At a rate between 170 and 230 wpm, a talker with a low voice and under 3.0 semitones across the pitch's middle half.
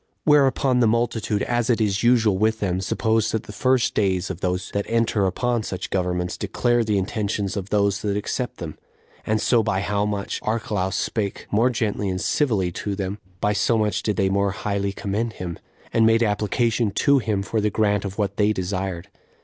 Yes: average, 200 wpm; low, 105 Hz; narrow, 2.5 semitones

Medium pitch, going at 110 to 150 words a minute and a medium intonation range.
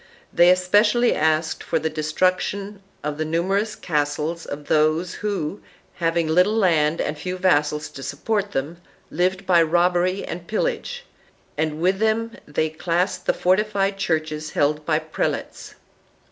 Yes: medium, 175 Hz; average, 145 wpm; average, 3.9 semitones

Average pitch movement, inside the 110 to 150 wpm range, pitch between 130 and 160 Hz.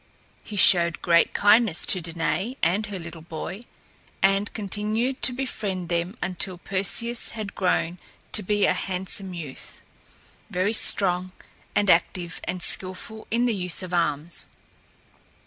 No: average, 3.2 semitones; slow, 135 wpm; medium, 185 Hz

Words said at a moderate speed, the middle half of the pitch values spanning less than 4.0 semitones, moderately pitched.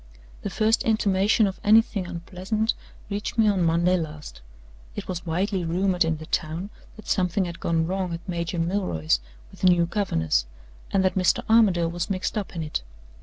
Yes: average, 175 wpm; average, 3.1 semitones; medium, 180 Hz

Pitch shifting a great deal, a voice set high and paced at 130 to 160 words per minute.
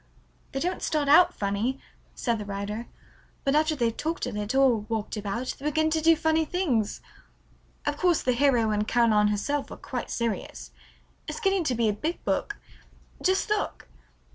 No: wide, 6.5 semitones; very high, 255 Hz; average, 175 wpm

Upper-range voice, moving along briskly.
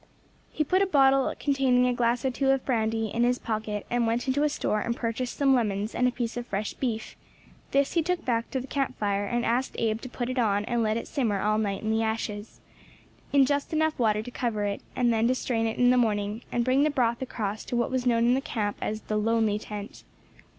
Yes: high, 235 Hz; fast, 245 wpm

